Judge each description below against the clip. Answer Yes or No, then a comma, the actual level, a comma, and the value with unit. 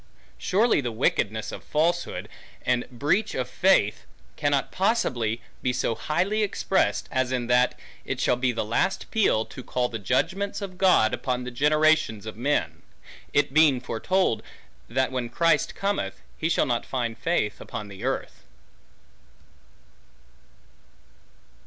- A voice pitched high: No, low, 130 Hz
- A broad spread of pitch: Yes, wide, 6.4 semitones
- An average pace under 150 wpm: Yes, average, 140 wpm